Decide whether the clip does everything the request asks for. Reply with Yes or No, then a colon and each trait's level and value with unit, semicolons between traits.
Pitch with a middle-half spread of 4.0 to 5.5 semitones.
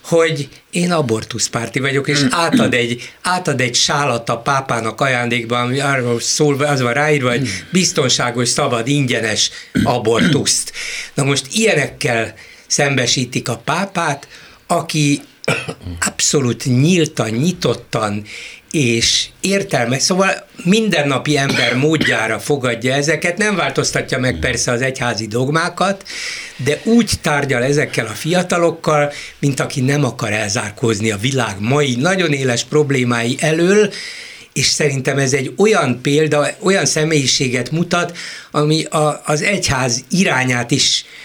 Yes: average, 4.9 semitones